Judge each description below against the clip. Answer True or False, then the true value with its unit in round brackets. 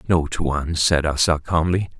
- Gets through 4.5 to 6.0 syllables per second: True (4.6 syllables/s)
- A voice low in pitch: True (80 Hz)